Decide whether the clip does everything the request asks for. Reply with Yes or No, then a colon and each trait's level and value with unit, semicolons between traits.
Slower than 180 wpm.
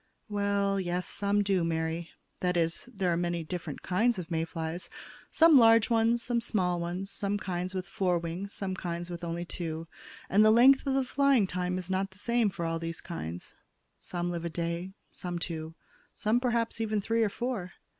No: average, 195 wpm